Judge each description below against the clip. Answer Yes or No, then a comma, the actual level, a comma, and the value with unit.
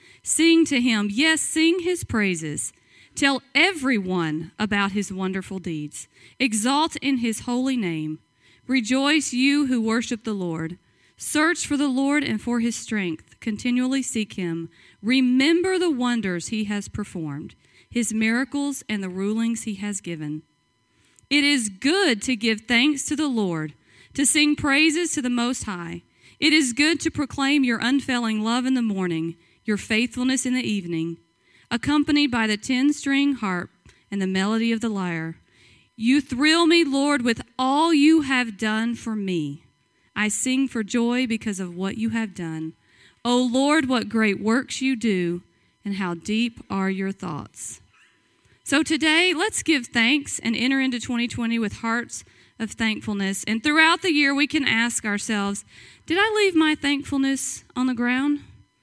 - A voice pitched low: No, high, 235 Hz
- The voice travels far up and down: Yes, wide, 5.8 semitones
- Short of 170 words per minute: Yes, average, 160 wpm